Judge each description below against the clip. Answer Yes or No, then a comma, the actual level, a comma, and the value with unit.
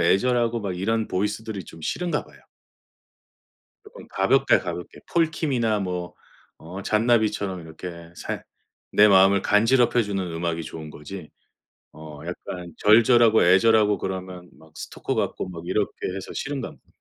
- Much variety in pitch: No, average, 4.2 semitones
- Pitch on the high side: No, low, 100 Hz